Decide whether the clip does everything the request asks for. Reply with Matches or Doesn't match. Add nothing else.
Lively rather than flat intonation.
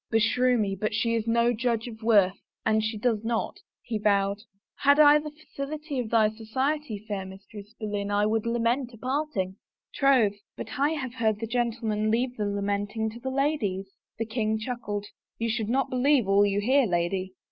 Doesn't match